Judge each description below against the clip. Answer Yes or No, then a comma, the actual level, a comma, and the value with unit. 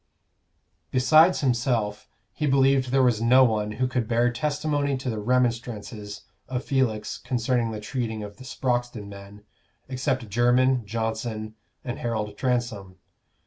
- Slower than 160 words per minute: Yes, slow, 135 wpm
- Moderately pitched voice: No, low, 120 Hz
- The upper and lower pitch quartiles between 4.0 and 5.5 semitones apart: No, average, 3.1 semitones